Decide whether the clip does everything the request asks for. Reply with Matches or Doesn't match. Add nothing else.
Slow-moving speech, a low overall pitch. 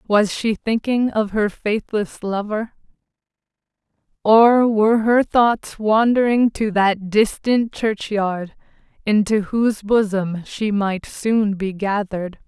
Doesn't match